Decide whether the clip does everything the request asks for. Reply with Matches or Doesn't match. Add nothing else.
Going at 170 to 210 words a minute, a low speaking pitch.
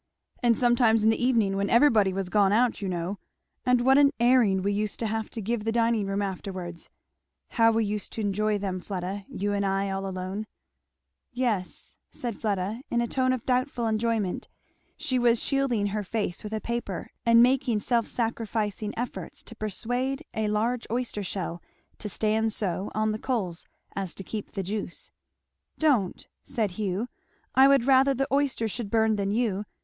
Doesn't match